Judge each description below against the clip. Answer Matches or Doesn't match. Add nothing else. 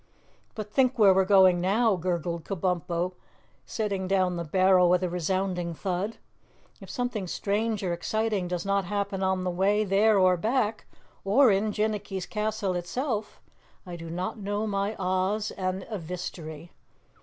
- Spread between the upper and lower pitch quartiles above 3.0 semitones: Doesn't match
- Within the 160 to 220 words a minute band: Doesn't match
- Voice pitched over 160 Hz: Matches